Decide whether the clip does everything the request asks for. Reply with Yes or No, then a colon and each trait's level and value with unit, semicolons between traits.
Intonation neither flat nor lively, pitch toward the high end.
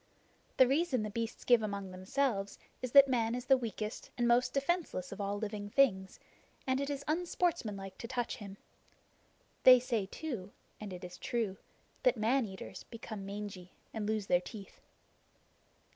Yes: average, 4.4 semitones; high, 225 Hz